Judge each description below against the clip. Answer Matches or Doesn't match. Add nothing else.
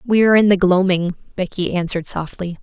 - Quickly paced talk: Doesn't match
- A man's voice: Doesn't match